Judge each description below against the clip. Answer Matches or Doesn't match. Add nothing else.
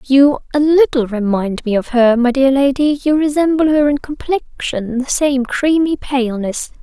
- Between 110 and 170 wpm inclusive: Matches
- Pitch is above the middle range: Matches